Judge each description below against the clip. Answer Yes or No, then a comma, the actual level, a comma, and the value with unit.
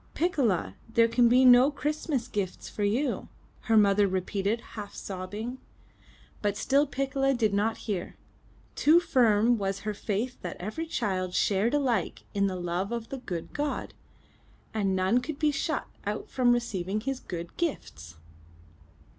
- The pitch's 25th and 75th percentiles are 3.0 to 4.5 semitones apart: No, average, 4.9 semitones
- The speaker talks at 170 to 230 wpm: No, average, 150 wpm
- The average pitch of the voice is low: No, high, 220 Hz